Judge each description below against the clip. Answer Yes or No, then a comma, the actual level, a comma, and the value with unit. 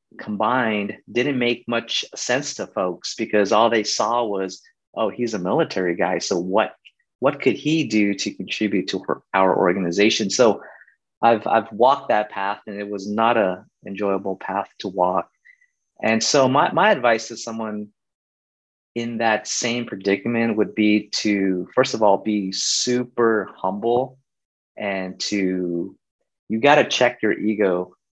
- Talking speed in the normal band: Yes, average, 155 wpm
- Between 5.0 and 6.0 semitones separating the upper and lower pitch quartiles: No, average, 2.7 semitones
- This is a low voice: Yes, low, 110 Hz